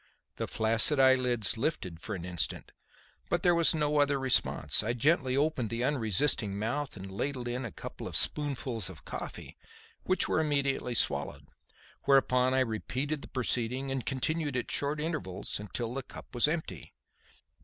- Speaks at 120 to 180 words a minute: Yes, average, 160 wpm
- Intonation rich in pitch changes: No, average, 4.5 semitones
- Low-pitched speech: Yes, low, 130 Hz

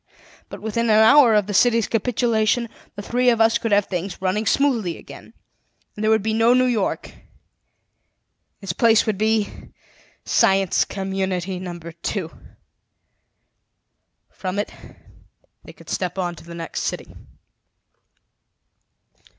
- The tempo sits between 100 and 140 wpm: Yes, slow, 135 wpm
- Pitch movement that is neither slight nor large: Yes, average, 3.2 semitones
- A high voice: Yes, high, 210 Hz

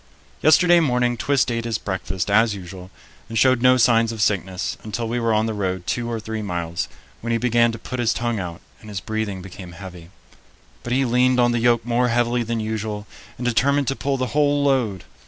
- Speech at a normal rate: No, fast, 210 wpm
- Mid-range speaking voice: No, low, 115 Hz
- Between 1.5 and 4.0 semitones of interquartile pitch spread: Yes, average, 3.2 semitones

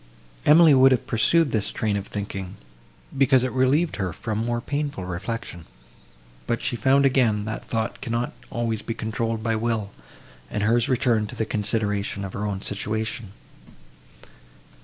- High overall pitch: No, low, 115 Hz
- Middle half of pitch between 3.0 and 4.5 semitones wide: Yes, average, 3.6 semitones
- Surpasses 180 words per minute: No, average, 155 wpm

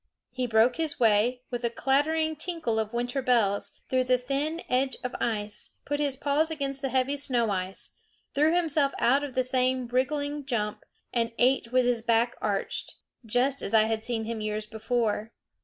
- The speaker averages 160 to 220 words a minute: Yes, average, 180 wpm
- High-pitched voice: Yes, very high, 250 Hz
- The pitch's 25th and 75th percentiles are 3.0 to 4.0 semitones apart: Yes, average, 3.6 semitones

